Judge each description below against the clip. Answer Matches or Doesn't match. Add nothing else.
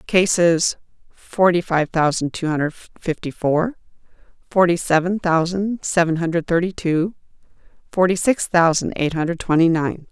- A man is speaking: Doesn't match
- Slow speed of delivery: Matches